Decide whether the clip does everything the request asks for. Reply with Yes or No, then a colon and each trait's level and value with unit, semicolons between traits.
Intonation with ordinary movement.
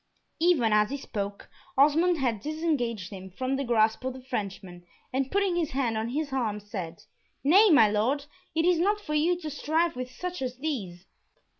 No: wide, 6.6 semitones